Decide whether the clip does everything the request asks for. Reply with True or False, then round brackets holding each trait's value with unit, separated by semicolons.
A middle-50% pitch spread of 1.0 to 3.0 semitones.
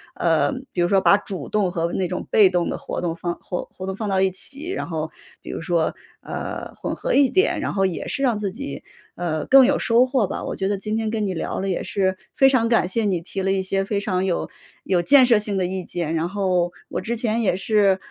False (3.7 semitones)